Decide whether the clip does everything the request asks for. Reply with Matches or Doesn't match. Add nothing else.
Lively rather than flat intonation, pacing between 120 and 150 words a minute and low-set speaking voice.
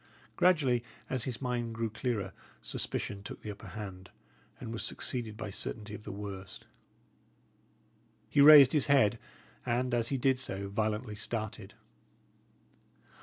Doesn't match